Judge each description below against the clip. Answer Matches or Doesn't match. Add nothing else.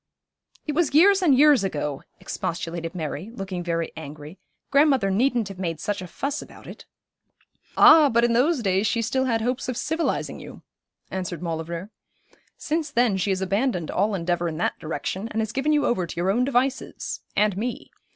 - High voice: Matches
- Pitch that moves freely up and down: Matches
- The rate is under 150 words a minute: Doesn't match